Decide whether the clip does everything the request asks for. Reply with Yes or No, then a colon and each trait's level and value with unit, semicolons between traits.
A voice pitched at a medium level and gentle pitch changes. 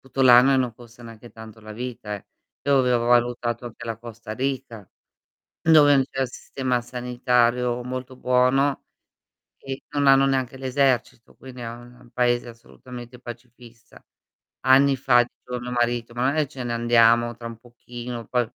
No: low, 125 Hz; narrow, 1.7 semitones